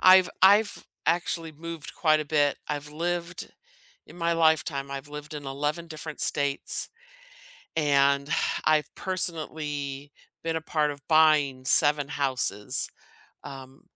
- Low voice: No, medium, 150 Hz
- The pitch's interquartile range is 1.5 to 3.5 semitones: Yes, narrow, 2.6 semitones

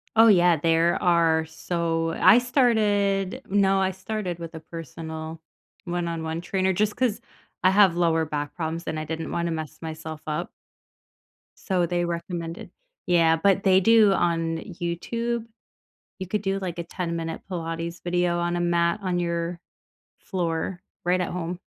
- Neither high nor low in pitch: Yes, medium, 175 Hz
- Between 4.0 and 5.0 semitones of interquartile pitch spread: No, narrow, 2.4 semitones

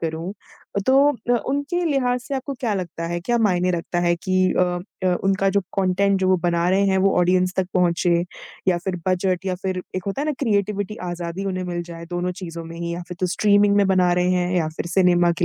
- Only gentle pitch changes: Yes, narrow, 2.2 semitones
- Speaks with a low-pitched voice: No, medium, 185 Hz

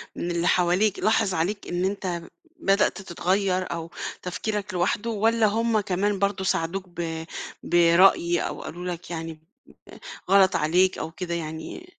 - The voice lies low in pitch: No, medium, 185 Hz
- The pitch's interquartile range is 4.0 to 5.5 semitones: No, average, 2.9 semitones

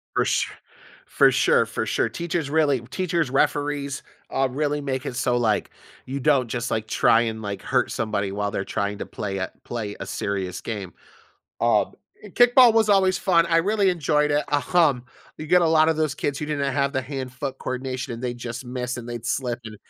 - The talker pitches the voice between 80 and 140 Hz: Yes, low, 135 Hz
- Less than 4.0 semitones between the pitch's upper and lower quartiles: No, average, 4.8 semitones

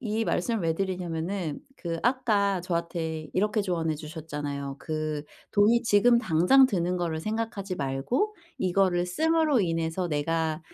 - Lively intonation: No, average, 4.7 semitones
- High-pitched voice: No, medium, 180 Hz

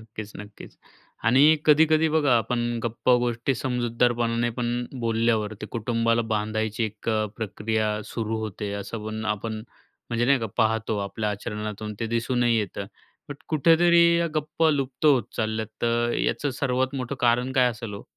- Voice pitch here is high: No, low, 115 Hz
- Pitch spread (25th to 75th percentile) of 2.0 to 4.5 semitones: Yes, narrow, 2.6 semitones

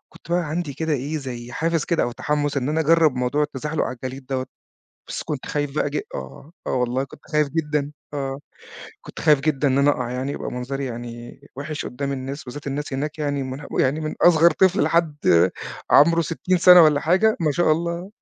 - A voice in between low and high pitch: Yes, medium, 145 Hz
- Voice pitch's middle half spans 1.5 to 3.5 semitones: Yes, average, 3.1 semitones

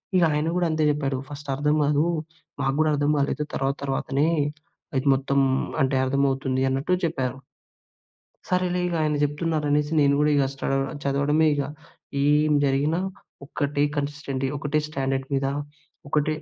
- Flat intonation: Yes, narrow, 1.8 semitones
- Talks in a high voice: No, medium, 145 Hz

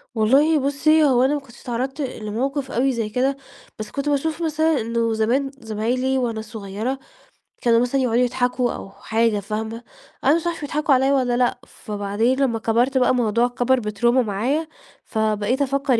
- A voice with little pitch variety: No, average, 3.5 semitones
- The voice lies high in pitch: Yes, very high, 250 Hz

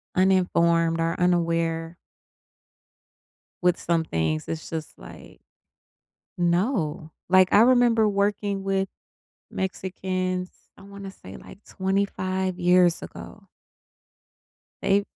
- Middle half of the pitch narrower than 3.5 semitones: Yes, average, 2.7 semitones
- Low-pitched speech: No, medium, 185 Hz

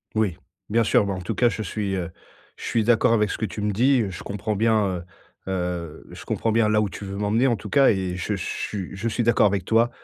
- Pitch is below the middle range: Yes, low, 105 Hz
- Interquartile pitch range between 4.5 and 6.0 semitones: No, average, 3.1 semitones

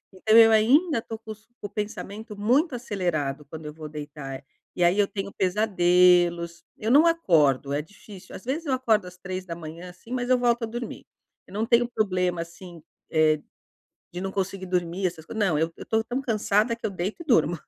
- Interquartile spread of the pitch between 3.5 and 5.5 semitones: Yes, average, 4.7 semitones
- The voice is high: Yes, high, 195 Hz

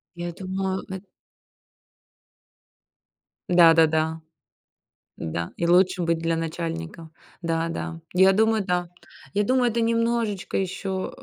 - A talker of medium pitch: Yes, medium, 180 Hz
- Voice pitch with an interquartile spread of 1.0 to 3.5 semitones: Yes, average, 2.9 semitones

